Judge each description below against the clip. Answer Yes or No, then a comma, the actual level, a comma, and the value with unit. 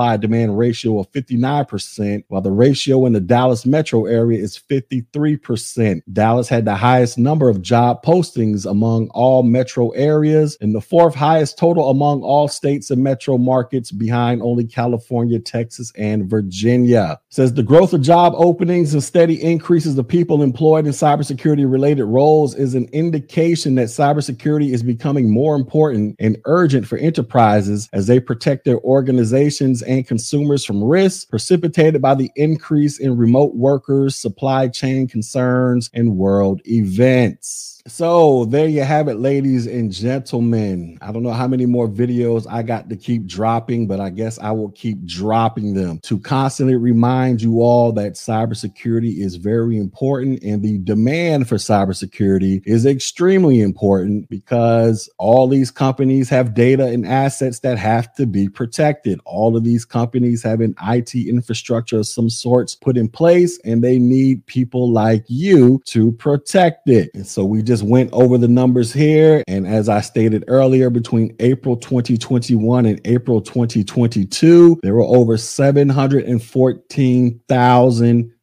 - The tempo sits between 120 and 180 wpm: Yes, average, 155 wpm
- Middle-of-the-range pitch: No, low, 125 Hz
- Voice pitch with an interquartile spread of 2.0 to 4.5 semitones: Yes, average, 3.3 semitones